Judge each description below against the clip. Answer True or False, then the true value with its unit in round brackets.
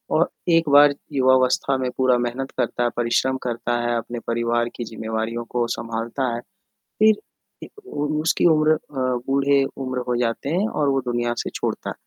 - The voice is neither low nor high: False (125 Hz)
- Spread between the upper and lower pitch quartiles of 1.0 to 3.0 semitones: True (2.7 semitones)